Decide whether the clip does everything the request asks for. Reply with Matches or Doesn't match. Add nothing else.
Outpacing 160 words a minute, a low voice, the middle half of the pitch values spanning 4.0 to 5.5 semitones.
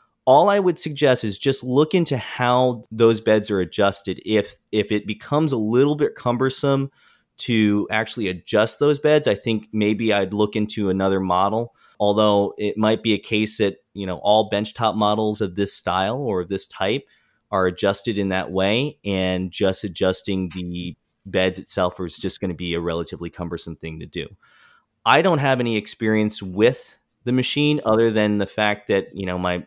Doesn't match